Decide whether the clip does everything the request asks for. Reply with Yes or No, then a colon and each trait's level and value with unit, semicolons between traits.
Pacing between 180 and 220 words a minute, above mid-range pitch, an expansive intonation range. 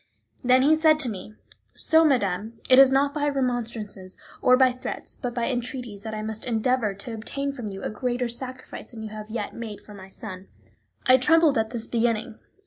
No: average, 200 wpm; high, 240 Hz; average, 3.2 semitones